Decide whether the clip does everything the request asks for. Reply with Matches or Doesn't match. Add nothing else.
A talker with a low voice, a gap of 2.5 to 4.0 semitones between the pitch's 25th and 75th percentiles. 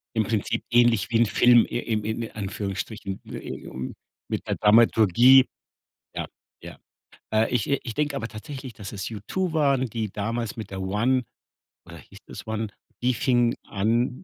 Matches